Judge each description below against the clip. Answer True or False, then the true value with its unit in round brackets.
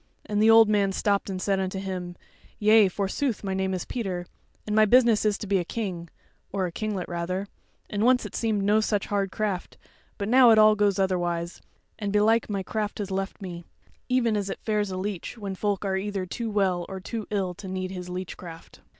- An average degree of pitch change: False (2.3 semitones)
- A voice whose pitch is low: False (200 Hz)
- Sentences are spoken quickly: True (220 wpm)